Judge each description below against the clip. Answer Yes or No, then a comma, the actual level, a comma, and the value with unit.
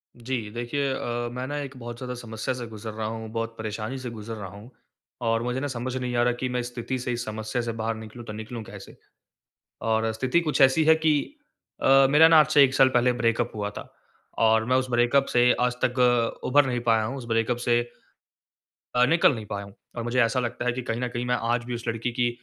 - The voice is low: Yes, low, 120 Hz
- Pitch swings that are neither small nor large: No, narrow, 2.1 semitones